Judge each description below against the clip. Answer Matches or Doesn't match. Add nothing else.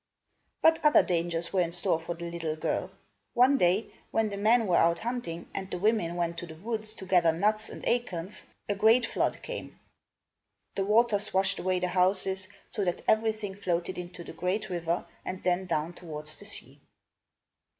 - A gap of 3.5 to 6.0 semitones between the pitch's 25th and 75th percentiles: Matches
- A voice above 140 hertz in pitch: Matches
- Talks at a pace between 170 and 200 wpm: Matches